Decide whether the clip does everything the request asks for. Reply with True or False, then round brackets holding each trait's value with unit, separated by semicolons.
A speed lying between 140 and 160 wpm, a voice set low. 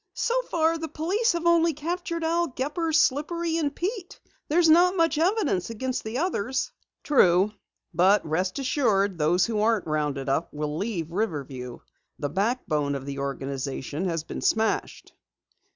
False (150 wpm; 230 Hz)